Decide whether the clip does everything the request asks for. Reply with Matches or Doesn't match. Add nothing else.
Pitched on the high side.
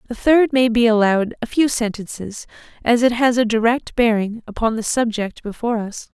Matches